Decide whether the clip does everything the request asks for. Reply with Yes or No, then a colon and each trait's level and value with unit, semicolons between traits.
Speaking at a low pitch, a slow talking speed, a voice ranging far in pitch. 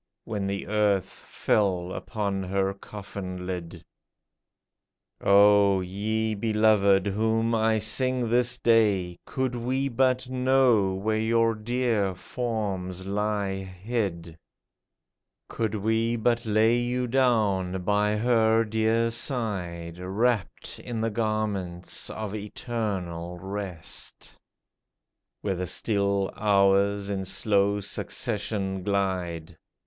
No: low, 105 Hz; slow, 100 wpm; average, 2.9 semitones